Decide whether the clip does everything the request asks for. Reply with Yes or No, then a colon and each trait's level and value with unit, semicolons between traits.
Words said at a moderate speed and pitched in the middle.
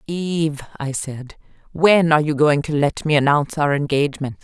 Yes: average, 175 wpm; medium, 150 Hz